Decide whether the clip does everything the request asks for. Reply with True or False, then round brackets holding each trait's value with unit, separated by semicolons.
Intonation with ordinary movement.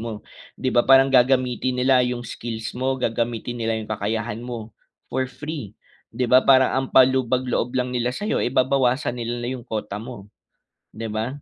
False (2.2 semitones)